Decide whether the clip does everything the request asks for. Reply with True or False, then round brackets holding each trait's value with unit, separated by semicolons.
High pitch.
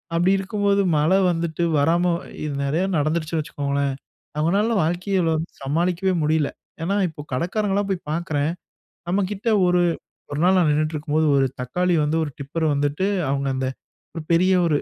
False (165 Hz)